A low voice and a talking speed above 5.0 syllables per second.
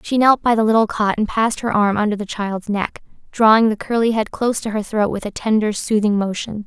No: high, 215 Hz; 5.8 syllables/s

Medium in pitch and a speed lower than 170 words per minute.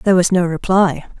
No: medium, 180 Hz; average, 200 wpm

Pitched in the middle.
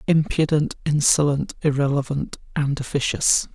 Yes: medium, 145 Hz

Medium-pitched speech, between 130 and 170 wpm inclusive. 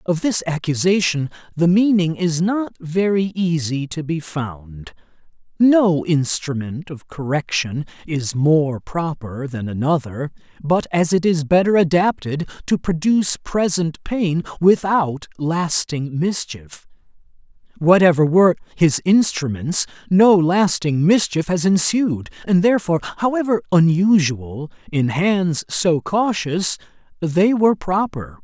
No: medium, 170 Hz; slow, 115 wpm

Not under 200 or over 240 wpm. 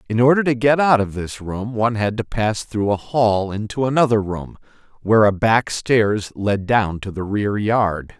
Yes: fast, 205 wpm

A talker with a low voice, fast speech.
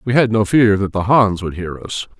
Yes: low, 105 Hz; fast, 275 wpm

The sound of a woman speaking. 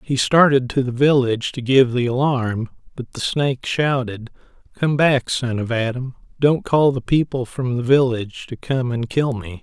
No: male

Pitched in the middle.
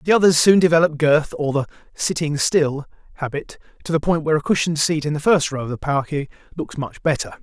Yes: medium, 150 Hz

